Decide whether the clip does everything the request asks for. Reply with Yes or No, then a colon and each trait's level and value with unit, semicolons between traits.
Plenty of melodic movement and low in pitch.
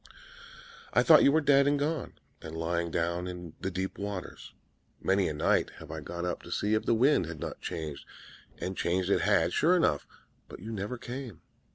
Yes: wide, 6.8 semitones; very low, 95 Hz